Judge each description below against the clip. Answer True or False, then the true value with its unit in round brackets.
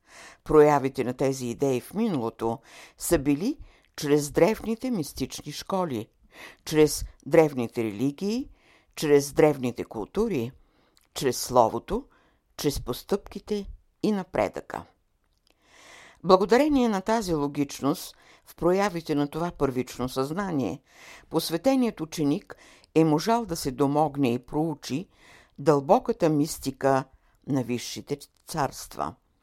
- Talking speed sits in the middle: False (100 wpm)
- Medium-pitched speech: True (150 Hz)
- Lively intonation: True (6.0 semitones)